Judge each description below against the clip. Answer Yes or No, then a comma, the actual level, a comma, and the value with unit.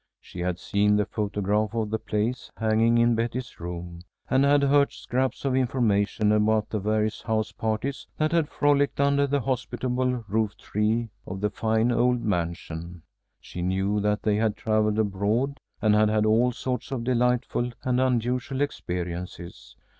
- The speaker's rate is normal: Yes, average, 155 wpm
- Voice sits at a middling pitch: No, low, 110 Hz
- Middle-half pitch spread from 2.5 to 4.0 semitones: Yes, average, 3.3 semitones